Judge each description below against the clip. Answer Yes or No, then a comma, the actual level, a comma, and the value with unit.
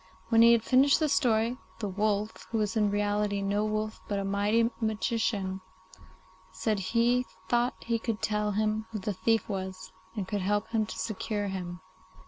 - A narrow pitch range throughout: Yes, narrow, 2.1 semitones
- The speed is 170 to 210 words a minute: Yes, average, 175 wpm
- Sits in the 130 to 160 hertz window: No, high, 215 Hz